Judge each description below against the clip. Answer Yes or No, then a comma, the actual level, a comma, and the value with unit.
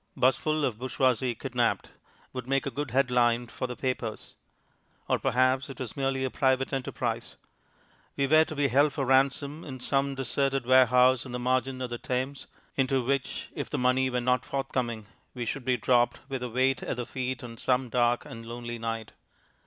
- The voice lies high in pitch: No, low, 130 Hz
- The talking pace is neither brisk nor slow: Yes, average, 190 wpm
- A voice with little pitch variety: Yes, narrow, 1.7 semitones